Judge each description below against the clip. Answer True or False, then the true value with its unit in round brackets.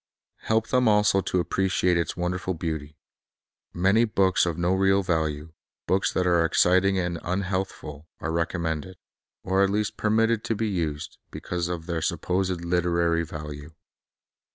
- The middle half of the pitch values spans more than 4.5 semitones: False (2.7 semitones)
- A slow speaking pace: False (150 wpm)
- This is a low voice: True (90 Hz)